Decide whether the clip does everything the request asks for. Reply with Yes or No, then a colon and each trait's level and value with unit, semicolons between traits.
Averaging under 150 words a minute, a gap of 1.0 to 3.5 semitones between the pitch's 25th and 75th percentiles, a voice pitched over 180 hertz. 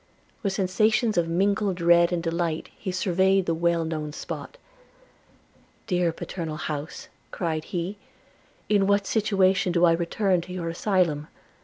No: average, 140 wpm; narrow, 2.6 semitones; medium, 175 Hz